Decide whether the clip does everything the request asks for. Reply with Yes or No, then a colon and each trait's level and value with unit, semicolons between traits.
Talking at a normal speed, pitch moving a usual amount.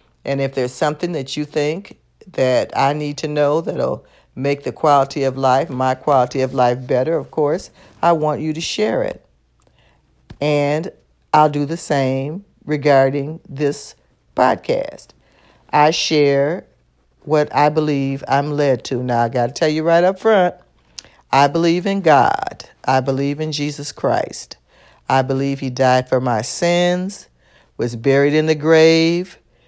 Yes: average, 155 wpm; average, 3.0 semitones